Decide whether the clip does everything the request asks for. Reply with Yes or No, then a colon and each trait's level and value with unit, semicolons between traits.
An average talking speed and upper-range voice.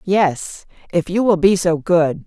No: average, 185 wpm; medium, 175 Hz